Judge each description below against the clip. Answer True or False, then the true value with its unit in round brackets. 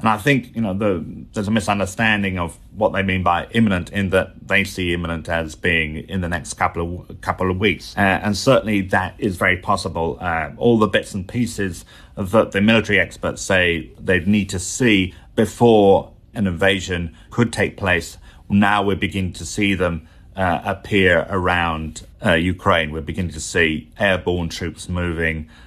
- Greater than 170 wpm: True (180 wpm)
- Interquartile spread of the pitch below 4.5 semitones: True (3.2 semitones)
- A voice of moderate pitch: False (95 Hz)